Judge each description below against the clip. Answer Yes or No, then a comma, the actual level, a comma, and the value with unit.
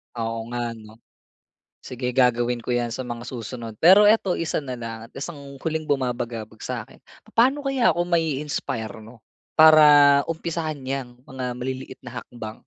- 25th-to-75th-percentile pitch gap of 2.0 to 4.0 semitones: No, average, 4.7 semitones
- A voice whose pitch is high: No, low, 130 Hz